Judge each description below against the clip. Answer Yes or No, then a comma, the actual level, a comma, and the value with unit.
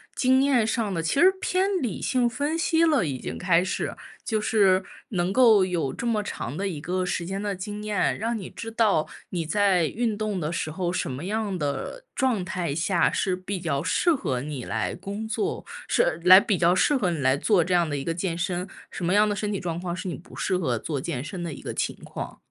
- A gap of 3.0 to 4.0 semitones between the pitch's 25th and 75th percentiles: No, average, 4.4 semitones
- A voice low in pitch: No, medium, 185 Hz